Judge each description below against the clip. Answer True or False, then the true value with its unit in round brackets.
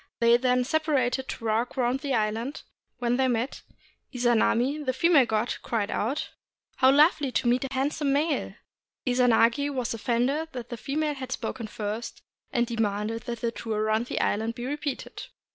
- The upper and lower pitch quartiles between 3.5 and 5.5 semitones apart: False (3.0 semitones)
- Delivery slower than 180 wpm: True (170 wpm)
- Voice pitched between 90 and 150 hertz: False (245 Hz)